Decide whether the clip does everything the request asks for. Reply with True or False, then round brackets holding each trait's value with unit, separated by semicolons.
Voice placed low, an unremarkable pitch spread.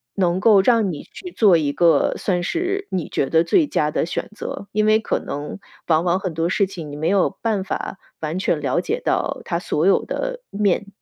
False (190 Hz; 4.3 semitones)